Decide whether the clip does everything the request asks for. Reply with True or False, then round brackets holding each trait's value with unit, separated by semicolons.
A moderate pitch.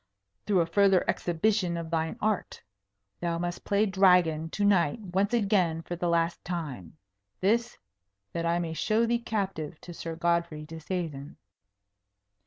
True (175 Hz)